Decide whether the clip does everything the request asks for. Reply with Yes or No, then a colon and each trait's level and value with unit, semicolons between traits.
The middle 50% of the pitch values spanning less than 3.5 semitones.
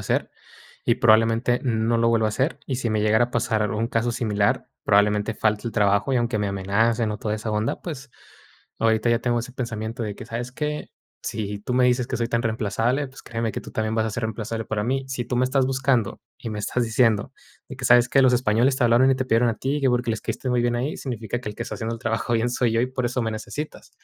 Yes: narrow, 2.4 semitones